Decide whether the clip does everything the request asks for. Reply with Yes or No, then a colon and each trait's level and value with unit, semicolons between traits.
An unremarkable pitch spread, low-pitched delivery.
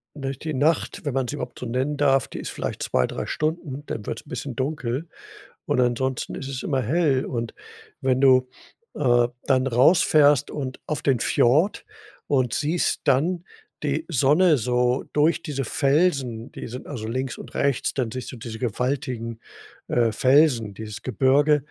Yes: average, 3.1 semitones; low, 130 Hz